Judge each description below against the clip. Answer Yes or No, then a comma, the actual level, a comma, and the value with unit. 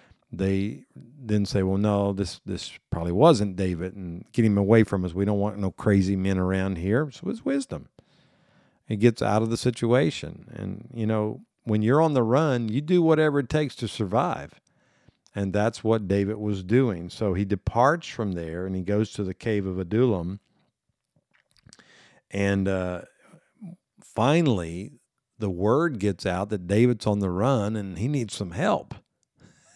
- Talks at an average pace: Yes, average, 170 wpm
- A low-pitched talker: Yes, low, 105 Hz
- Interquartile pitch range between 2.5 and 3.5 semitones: No, average, 3.9 semitones